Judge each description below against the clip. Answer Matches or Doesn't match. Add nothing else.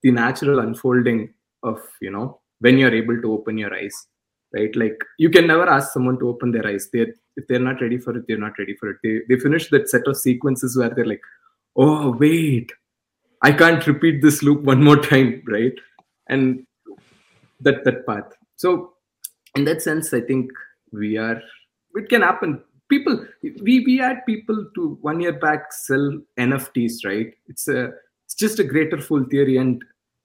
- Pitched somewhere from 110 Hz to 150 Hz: Matches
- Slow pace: Doesn't match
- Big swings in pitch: Doesn't match